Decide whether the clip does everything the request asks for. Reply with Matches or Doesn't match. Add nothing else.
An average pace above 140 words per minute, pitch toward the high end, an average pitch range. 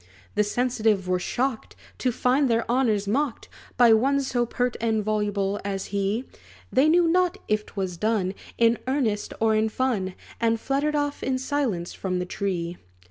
Matches